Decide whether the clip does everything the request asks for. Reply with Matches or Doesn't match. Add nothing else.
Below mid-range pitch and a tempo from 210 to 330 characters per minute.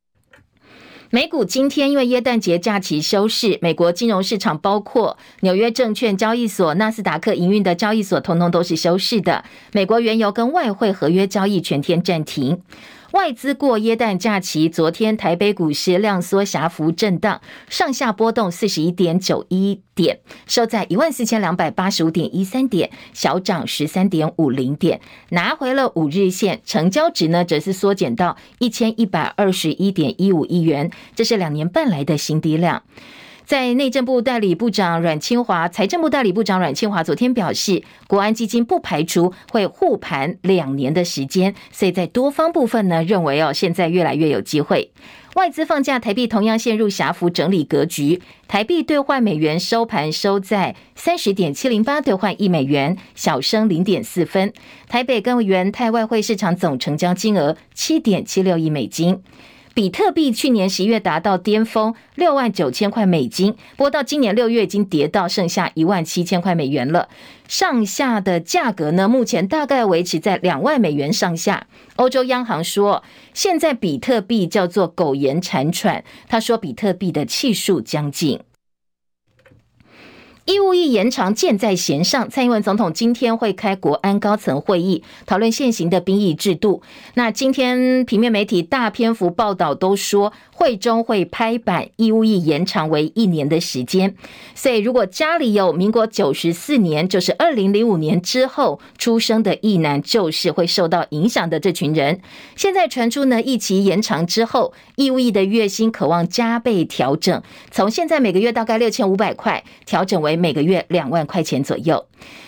Doesn't match